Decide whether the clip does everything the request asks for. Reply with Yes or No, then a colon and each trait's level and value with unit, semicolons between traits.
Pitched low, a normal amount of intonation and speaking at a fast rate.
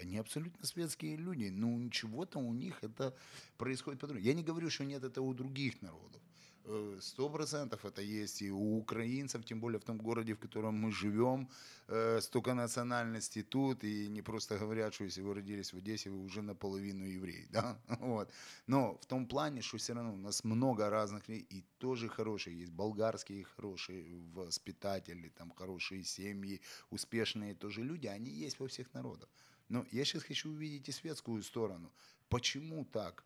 Yes: low, 110 Hz; average, 4.5 semitones; fast, 170 wpm